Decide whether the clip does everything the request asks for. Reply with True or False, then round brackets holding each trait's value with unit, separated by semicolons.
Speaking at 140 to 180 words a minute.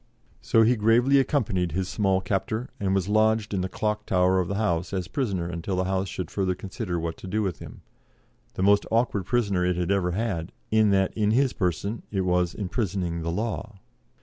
False (205 wpm)